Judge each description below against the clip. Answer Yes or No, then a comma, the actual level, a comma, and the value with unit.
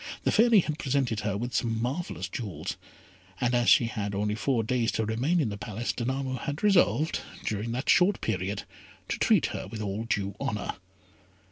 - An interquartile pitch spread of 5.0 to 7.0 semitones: No, average, 4.4 semitones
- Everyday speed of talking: Yes, average, 180 wpm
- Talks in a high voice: No, low, 115 Hz